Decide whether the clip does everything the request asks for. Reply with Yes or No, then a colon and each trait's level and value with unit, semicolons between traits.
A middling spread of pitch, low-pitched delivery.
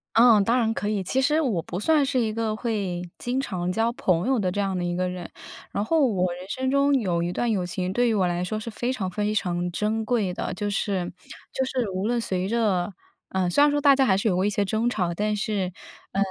No: average, 4.6 semitones; high, 210 Hz